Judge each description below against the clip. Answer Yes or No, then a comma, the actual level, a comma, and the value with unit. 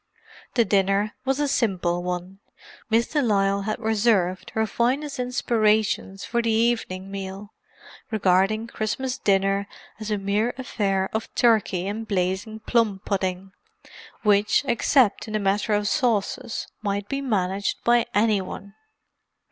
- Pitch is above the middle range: Yes, high, 210 Hz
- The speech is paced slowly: Yes, slow, 130 wpm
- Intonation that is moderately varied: Yes, average, 3.0 semitones